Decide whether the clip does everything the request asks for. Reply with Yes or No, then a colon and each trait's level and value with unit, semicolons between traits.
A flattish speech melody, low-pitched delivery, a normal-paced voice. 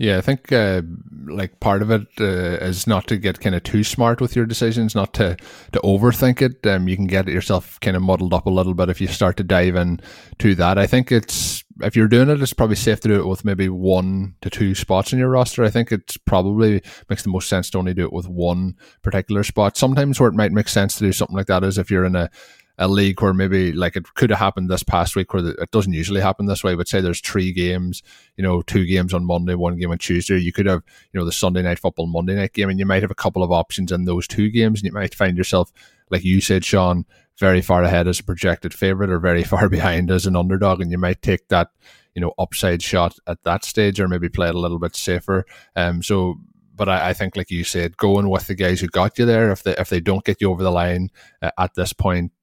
No: narrow, 2.3 semitones; very low, 95 Hz; fast, 265 wpm